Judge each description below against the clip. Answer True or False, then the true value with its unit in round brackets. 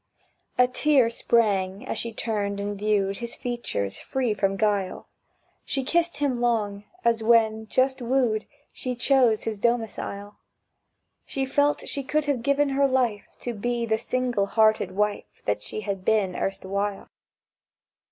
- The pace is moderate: True (145 wpm)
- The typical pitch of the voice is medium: False (225 Hz)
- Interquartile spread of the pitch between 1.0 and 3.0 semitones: False (3.7 semitones)